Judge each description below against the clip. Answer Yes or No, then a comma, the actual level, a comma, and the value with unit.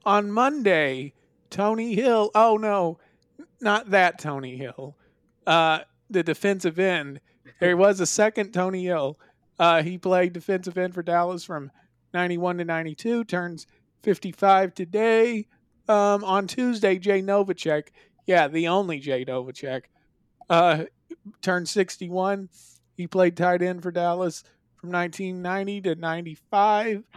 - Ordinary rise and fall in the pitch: Yes, average, 3.5 semitones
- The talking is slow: Yes, slow, 125 wpm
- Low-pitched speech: No, medium, 180 Hz